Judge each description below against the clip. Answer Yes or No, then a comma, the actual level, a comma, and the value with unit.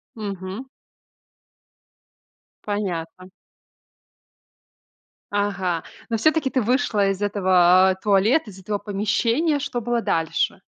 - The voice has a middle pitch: No, high, 205 Hz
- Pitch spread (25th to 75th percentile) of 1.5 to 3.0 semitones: No, average, 3.7 semitones